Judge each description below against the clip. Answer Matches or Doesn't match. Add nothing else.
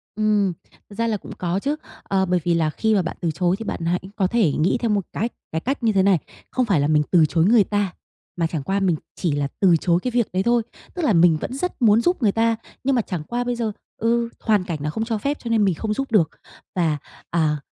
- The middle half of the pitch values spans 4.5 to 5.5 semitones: Matches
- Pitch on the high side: Matches